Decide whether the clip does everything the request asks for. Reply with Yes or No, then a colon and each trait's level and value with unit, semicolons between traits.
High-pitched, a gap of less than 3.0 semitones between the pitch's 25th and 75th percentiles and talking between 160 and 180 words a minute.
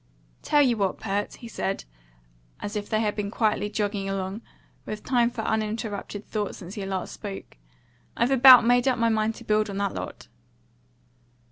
Yes: high, 215 Hz; narrow, 2.4 semitones; average, 175 wpm